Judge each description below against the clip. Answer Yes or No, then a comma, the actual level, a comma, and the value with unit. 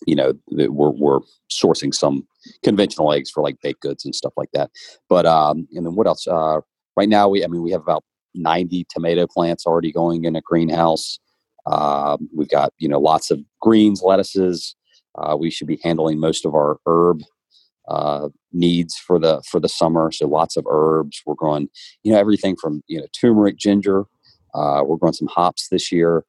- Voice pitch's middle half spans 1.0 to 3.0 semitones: Yes, narrow, 2.6 semitones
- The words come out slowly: No, average, 195 wpm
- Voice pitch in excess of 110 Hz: No, very low, 85 Hz